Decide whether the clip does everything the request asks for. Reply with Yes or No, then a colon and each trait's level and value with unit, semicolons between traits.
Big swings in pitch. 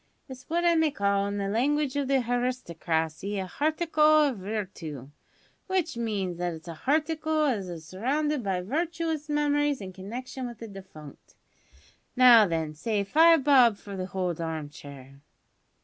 Yes: wide, 8.0 semitones